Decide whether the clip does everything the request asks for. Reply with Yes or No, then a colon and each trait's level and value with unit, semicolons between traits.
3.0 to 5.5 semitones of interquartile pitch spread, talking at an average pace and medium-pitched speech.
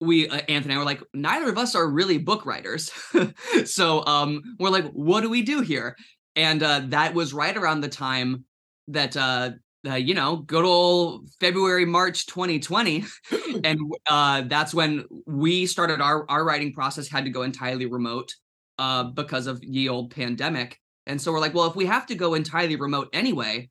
Yes: average, 4.4 semitones; average, 190 wpm; medium, 150 Hz